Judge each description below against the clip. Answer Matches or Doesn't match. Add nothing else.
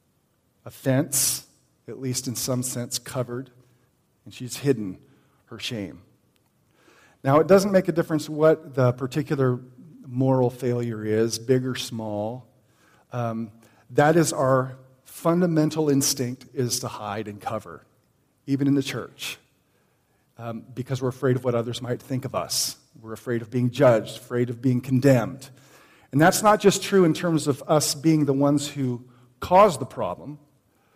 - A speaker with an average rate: Matches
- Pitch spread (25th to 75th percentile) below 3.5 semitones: Matches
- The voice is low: Matches